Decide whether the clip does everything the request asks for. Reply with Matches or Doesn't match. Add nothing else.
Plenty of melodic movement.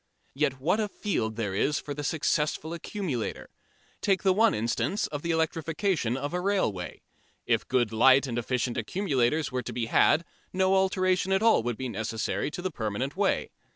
Matches